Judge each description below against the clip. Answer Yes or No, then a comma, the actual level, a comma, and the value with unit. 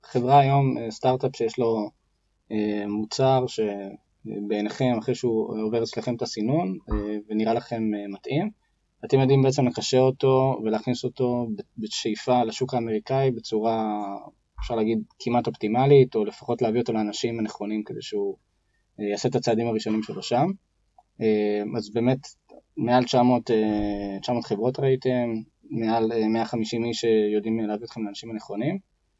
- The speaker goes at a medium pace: Yes, average, 135 wpm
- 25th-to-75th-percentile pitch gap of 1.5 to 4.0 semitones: Yes, average, 2.8 semitones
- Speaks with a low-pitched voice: Yes, low, 115 Hz